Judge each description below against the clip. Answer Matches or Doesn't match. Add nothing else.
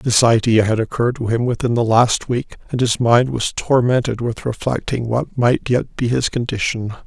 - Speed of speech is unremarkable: Matches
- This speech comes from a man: Matches